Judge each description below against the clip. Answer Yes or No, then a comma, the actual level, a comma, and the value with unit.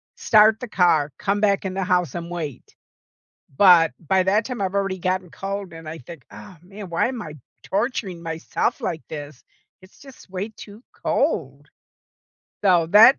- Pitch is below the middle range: No, medium, 185 Hz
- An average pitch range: Yes, average, 3.6 semitones